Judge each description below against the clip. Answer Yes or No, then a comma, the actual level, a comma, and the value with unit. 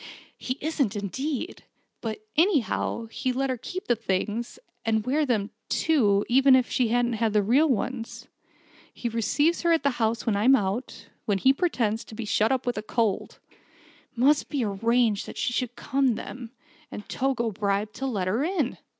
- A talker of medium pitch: No, high, 240 Hz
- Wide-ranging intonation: No, average, 3.7 semitones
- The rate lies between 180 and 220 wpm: Yes, average, 185 wpm